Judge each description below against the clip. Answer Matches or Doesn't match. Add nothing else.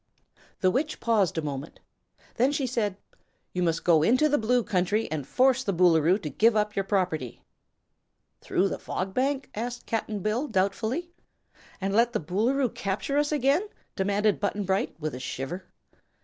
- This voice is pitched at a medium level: Doesn't match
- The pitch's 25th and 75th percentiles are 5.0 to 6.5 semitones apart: Matches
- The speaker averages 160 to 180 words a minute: Matches